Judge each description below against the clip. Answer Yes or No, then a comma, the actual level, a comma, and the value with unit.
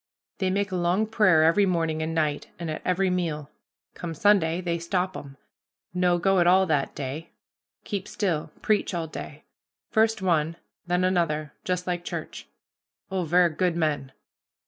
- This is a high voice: No, medium, 175 Hz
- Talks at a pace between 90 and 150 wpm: No, average, 165 wpm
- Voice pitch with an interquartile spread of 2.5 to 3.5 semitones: Yes, average, 2.8 semitones